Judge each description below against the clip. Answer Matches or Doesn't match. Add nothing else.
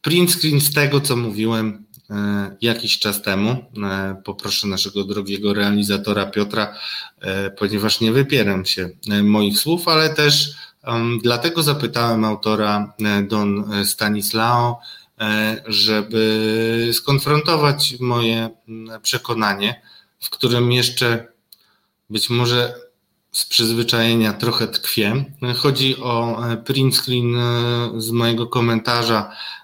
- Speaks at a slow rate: Matches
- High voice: Doesn't match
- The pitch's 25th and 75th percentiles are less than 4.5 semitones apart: Matches